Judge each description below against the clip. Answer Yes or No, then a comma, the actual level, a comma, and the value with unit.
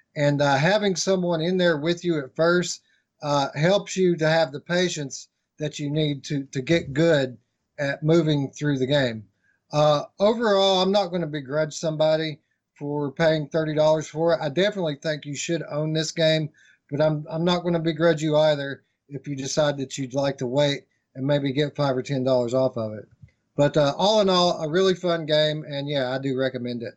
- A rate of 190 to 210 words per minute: Yes, fast, 205 wpm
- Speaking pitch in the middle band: Yes, medium, 150 Hz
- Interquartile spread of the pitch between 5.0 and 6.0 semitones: No, average, 3.2 semitones